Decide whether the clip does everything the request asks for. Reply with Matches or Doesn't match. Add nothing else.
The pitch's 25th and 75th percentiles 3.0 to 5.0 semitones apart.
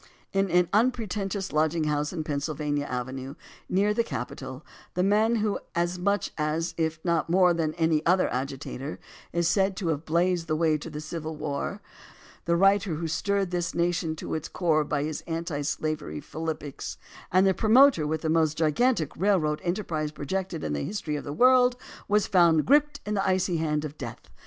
Matches